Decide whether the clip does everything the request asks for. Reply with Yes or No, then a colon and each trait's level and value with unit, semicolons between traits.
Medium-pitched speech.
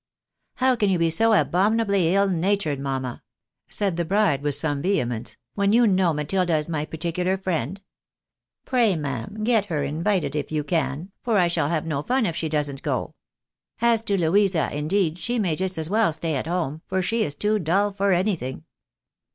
Yes: medium, 175 Hz